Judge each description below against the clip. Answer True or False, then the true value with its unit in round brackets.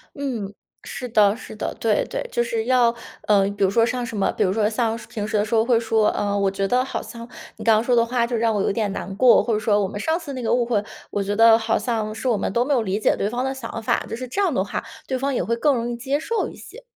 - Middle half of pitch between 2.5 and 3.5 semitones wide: True (2.9 semitones)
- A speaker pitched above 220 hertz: True (230 Hz)